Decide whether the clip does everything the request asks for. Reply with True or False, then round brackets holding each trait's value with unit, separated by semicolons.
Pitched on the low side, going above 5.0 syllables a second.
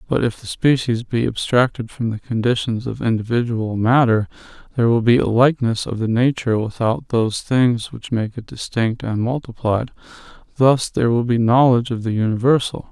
True (120 Hz; 5.4 syllables/s)